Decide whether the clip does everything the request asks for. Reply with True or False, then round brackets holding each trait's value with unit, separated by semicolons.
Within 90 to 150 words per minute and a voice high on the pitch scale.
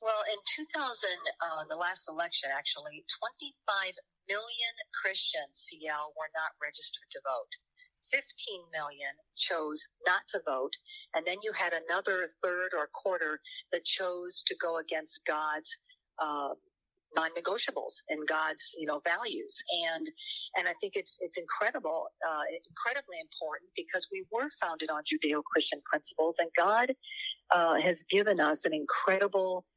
True (140 wpm; 195 Hz)